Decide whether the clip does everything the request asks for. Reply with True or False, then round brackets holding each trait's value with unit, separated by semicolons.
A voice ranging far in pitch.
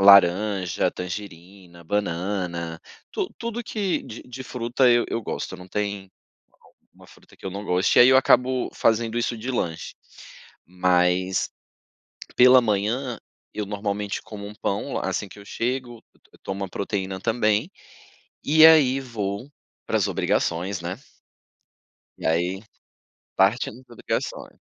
False (4.5 semitones)